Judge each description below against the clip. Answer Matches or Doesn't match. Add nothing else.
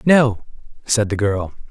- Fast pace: Doesn't match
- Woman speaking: Doesn't match